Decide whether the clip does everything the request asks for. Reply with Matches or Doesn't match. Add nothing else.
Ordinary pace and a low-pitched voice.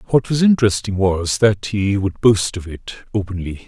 Matches